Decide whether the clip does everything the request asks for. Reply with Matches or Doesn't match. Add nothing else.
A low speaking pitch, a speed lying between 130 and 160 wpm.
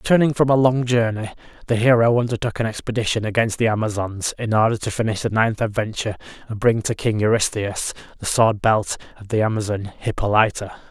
Doesn't match